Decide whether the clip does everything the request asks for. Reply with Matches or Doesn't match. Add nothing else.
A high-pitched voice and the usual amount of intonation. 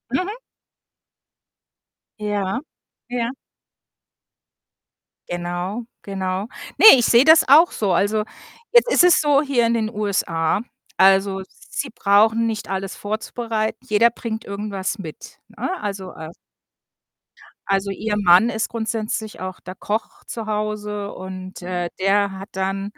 Matches